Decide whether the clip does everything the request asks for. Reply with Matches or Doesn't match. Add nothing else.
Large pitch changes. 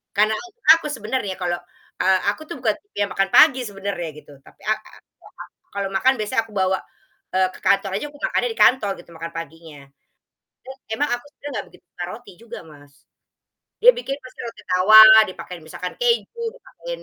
Matches